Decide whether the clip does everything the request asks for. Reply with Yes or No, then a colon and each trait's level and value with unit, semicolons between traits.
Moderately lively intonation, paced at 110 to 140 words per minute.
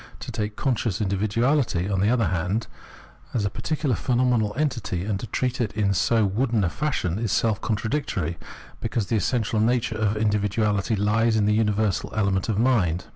No: average, 3.0 semitones; average, 170 wpm